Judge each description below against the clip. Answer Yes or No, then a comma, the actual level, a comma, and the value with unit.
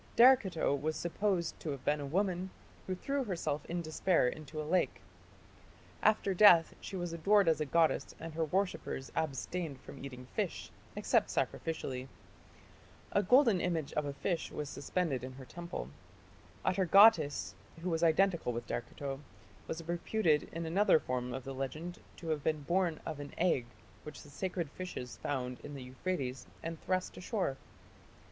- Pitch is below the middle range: No, medium, 160 Hz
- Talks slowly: No, average, 165 wpm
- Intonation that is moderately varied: Yes, average, 4.5 semitones